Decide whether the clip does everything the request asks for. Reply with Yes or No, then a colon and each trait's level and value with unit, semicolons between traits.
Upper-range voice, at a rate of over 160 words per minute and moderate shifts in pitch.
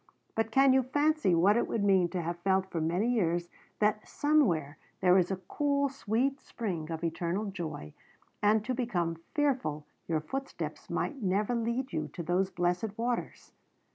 No: high, 200 Hz; average, 170 wpm; wide, 6.1 semitones